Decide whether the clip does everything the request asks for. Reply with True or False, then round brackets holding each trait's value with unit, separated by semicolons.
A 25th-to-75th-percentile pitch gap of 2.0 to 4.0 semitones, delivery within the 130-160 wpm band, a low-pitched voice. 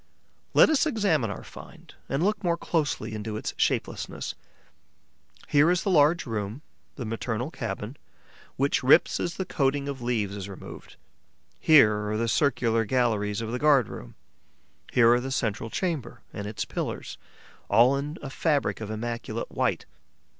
False (5.2 semitones; 155 wpm; 125 Hz)